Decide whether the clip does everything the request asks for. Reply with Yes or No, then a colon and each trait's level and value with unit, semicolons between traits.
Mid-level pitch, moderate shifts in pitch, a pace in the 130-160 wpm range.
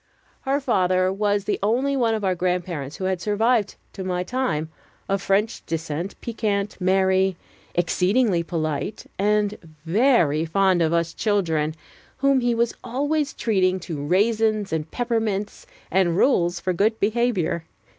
No: high, 195 Hz; average, 4.4 semitones; average, 140 wpm